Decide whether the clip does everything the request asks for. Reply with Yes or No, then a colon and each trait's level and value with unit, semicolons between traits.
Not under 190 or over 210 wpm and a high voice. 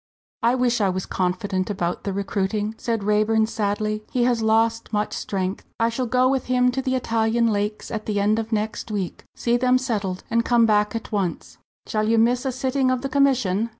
Yes: fast, 205 wpm; high, 225 Hz